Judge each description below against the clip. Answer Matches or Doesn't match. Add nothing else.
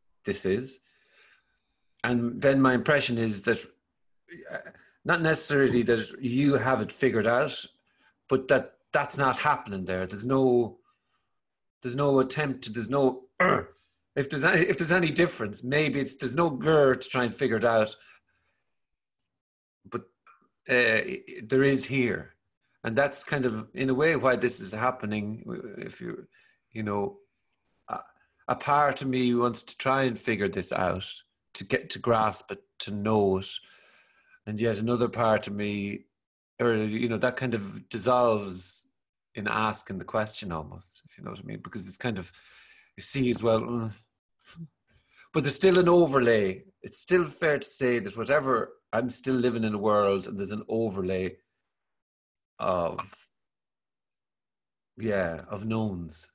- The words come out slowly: Doesn't match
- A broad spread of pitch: Doesn't match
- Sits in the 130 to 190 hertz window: Doesn't match